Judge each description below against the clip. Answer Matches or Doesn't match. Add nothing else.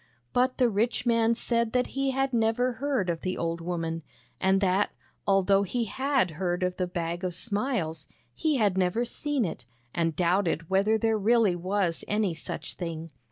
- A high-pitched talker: Matches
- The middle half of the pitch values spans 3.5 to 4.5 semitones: Doesn't match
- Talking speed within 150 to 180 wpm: Matches